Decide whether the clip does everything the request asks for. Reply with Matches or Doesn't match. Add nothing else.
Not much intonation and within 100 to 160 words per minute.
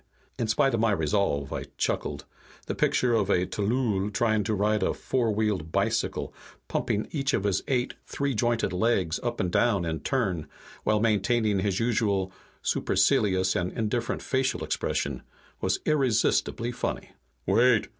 Doesn't match